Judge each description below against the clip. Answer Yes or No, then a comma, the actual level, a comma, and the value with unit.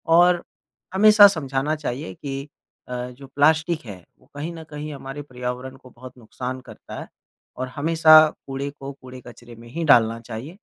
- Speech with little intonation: No, average, 4.0 semitones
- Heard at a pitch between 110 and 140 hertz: Yes, low, 135 Hz